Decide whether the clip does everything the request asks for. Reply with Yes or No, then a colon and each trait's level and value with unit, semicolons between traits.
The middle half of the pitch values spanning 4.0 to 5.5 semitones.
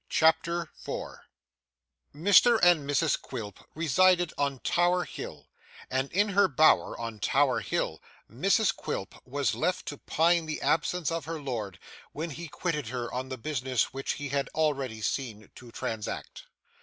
Yes: average, 4.7 semitones